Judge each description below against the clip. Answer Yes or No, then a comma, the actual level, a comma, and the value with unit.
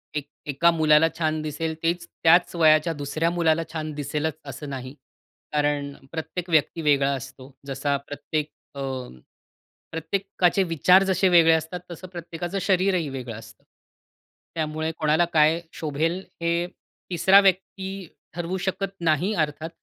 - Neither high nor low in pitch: Yes, medium, 160 Hz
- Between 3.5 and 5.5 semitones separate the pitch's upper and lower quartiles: No, average, 2.8 semitones